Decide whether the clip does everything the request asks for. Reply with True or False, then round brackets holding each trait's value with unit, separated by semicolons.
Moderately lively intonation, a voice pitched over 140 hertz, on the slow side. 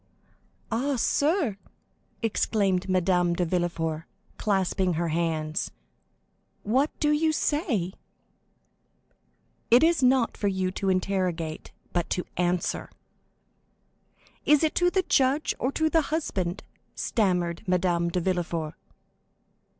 False (7.4 semitones; 190 Hz; 110 wpm)